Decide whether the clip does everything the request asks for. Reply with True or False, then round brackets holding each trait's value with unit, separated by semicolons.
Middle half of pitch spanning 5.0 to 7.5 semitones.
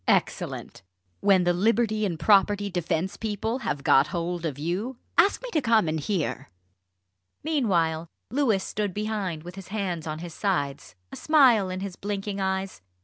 False (4.2 semitones)